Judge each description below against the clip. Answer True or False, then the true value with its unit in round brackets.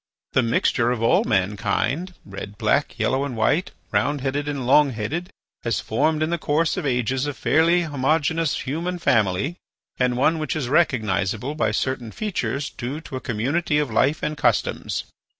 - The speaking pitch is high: False (140 Hz)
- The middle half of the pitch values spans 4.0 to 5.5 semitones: True (4.9 semitones)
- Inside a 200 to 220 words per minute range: False (170 wpm)